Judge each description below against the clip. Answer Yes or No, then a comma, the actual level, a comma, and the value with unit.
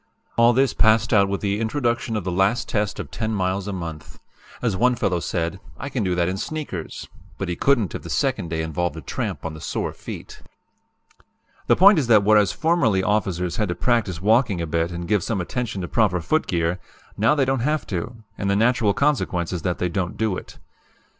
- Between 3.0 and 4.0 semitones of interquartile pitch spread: No, average, 4.9 semitones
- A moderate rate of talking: No, fast, 210 wpm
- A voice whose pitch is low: Yes, low, 100 Hz